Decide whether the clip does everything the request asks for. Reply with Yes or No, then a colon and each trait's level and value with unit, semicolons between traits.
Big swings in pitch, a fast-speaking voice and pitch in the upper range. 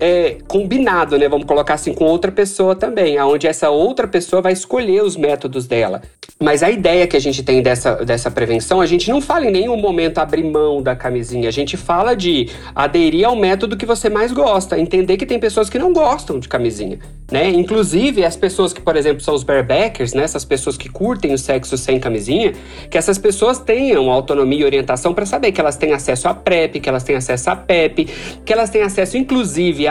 No: wide, 7.3 semitones; fast, 210 wpm; medium, 175 Hz